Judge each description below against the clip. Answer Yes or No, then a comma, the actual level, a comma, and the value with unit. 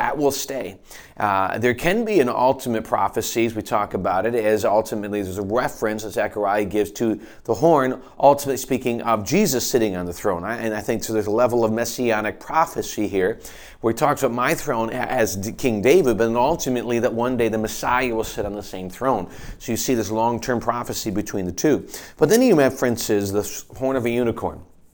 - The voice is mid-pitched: No, low, 115 Hz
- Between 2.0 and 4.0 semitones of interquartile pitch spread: Yes, average, 2.8 semitones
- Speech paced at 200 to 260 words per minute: Yes, fast, 205 wpm